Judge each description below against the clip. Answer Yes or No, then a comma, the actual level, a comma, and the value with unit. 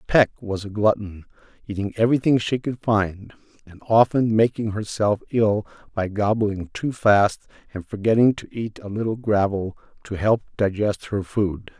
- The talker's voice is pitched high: No, low, 105 Hz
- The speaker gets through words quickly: No, average, 155 wpm